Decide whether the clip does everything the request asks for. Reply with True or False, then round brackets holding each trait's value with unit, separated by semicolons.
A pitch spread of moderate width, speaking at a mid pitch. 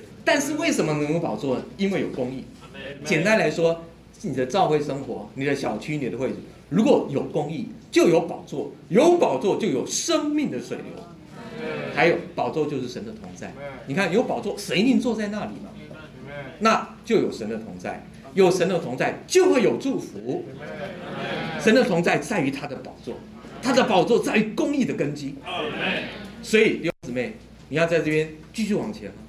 False (7.4 semitones; 170 Hz)